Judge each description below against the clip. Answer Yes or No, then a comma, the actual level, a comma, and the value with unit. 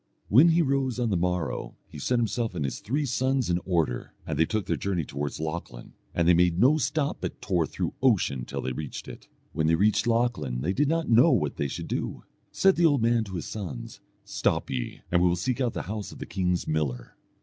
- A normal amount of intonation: No, wide, 7.3 semitones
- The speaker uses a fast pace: Yes, fast, 230 wpm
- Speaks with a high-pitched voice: No, very low, 95 Hz